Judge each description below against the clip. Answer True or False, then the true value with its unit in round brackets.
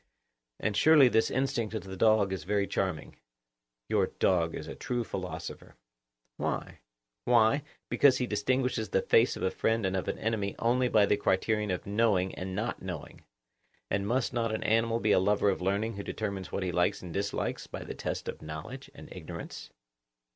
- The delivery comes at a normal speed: True (185 wpm)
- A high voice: False (105 Hz)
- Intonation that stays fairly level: False (3.5 semitones)